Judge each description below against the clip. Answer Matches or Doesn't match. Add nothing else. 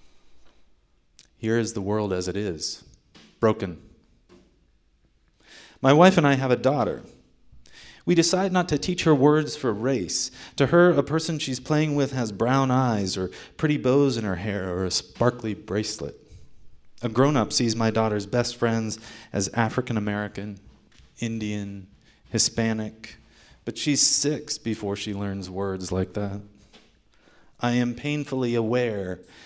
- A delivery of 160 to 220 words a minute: Doesn't match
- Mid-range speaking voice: Doesn't match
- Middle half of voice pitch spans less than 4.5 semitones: Doesn't match